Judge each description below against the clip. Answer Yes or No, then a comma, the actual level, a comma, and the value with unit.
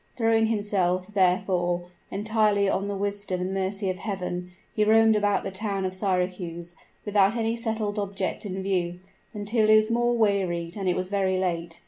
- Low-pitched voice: No, high, 195 Hz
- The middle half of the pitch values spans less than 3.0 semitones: Yes, narrow, 2.6 semitones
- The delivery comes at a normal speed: Yes, average, 170 wpm